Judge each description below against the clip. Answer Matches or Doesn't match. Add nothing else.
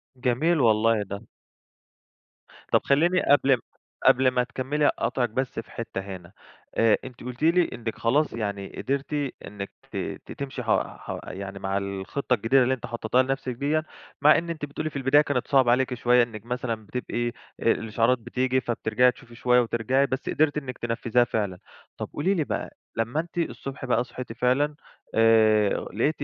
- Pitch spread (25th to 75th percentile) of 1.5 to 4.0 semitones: Matches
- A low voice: Matches